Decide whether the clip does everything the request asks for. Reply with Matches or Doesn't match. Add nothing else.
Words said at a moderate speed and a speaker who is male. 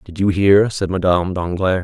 Matches